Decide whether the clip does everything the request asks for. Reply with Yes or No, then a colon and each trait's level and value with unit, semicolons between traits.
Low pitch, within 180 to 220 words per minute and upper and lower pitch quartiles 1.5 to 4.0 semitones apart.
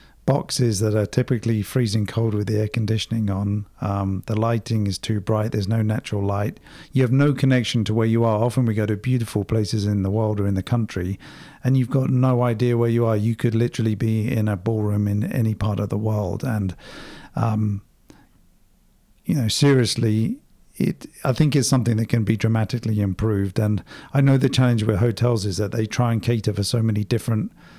Yes: low, 110 Hz; fast, 205 wpm; narrow, 2.5 semitones